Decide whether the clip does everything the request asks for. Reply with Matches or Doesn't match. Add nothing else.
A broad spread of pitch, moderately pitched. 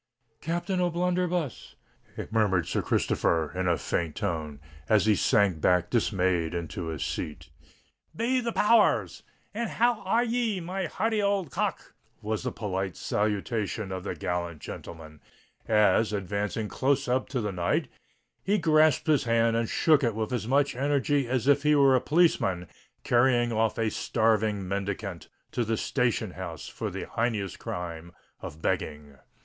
Doesn't match